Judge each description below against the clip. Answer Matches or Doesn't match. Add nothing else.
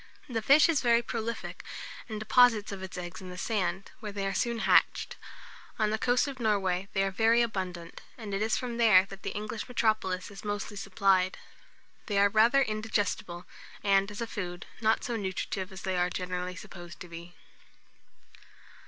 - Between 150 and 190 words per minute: Matches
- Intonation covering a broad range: Doesn't match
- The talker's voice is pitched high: Matches